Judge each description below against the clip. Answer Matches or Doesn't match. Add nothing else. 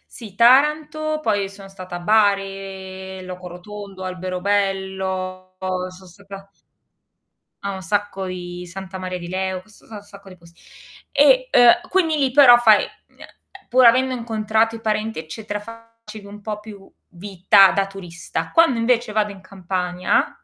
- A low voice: Doesn't match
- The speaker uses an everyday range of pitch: Matches